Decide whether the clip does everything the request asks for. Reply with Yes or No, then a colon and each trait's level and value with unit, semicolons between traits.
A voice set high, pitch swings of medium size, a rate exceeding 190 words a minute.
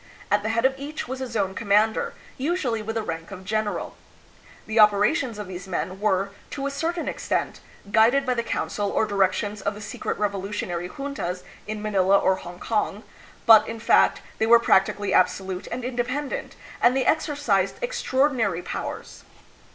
No: high, 215 Hz; average, 4.3 semitones; average, 165 wpm